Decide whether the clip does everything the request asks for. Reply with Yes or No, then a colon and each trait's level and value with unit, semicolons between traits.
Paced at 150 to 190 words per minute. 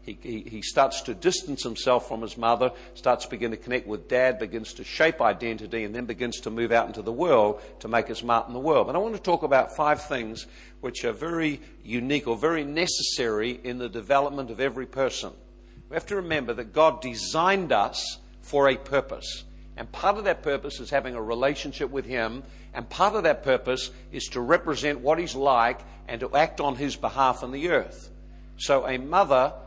No: fast, 205 wpm